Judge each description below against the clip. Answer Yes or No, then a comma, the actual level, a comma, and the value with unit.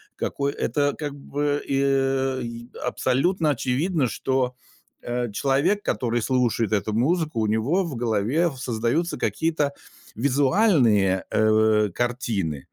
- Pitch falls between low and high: No, low, 130 Hz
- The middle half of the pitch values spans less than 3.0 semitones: No, average, 4.1 semitones